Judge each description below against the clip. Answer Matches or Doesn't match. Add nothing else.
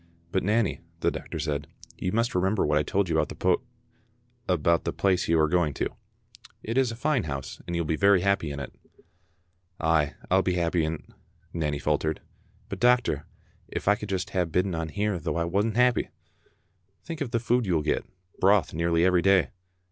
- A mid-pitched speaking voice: Doesn't match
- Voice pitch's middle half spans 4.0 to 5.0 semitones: Matches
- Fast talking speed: Matches